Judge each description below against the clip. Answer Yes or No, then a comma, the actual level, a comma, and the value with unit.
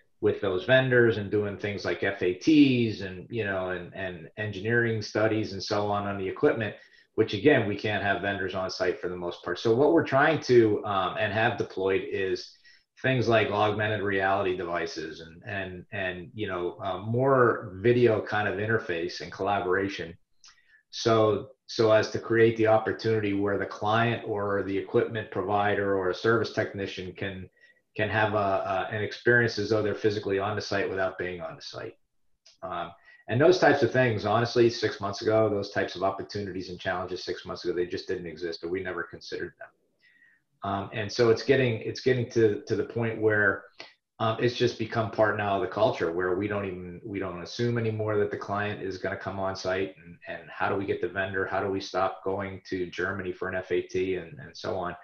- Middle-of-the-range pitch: No, low, 105 Hz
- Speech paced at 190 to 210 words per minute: Yes, fast, 205 wpm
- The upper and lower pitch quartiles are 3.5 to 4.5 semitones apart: No, average, 3.1 semitones